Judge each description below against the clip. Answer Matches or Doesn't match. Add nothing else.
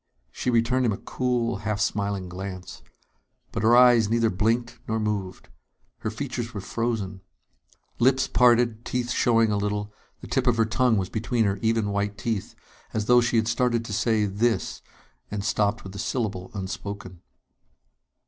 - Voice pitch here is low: Matches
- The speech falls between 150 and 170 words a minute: Matches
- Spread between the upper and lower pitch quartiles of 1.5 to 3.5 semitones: Matches